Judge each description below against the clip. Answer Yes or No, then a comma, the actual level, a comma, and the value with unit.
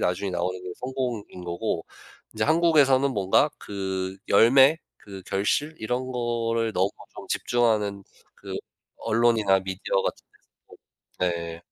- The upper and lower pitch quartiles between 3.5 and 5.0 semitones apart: Yes, average, 4.6 semitones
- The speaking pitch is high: No, low, 105 Hz